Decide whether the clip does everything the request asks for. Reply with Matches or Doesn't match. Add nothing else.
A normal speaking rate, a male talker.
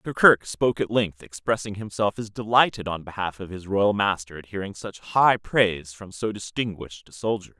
Matches